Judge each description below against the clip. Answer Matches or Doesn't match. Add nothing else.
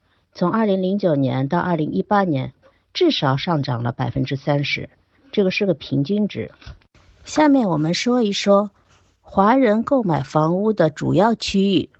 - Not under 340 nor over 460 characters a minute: Doesn't match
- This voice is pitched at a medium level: Matches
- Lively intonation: Matches